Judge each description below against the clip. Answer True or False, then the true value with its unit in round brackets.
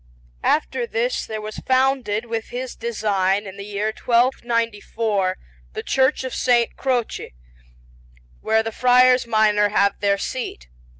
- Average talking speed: False (130 wpm)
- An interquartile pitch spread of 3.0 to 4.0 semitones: True (3.4 semitones)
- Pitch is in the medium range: False (225 Hz)